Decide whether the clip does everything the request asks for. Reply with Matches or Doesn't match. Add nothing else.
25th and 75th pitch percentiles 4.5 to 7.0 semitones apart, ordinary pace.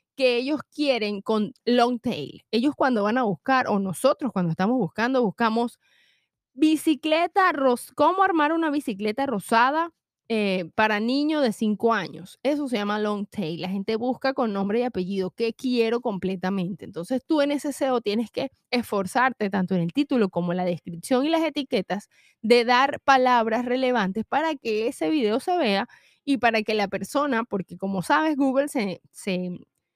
Matches